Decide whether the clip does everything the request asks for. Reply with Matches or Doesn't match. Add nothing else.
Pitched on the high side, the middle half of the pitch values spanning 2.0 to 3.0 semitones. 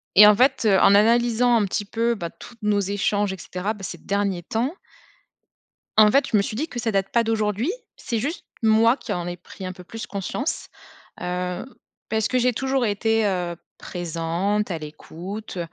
Doesn't match